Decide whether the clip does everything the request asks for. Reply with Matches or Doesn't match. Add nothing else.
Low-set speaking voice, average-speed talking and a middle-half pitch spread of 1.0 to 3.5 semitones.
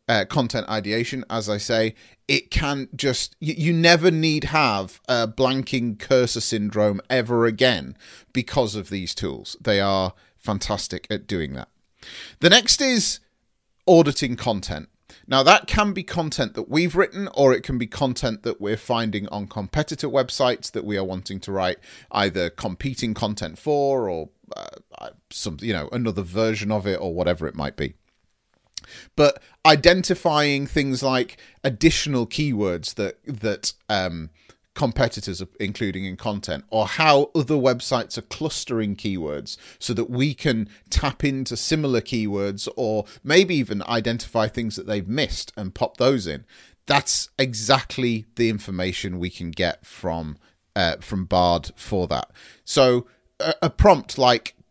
Doesn't match